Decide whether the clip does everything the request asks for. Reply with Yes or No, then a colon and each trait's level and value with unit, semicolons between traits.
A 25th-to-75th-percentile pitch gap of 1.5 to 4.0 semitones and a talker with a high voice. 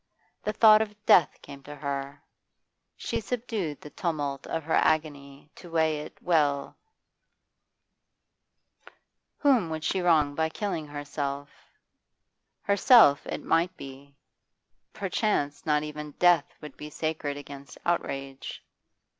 No: average, 3.7 semitones; medium, 150 Hz